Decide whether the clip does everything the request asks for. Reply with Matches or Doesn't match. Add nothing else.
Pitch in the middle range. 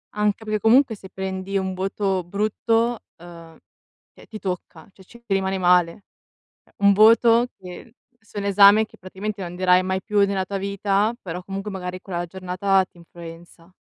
Doesn't match